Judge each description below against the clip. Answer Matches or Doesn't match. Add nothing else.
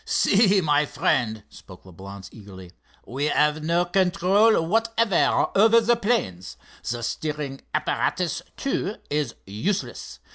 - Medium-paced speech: Doesn't match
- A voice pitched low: Doesn't match